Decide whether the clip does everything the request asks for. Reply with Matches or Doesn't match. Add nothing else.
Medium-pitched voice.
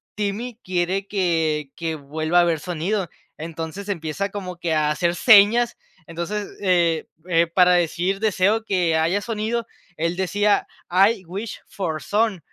Matches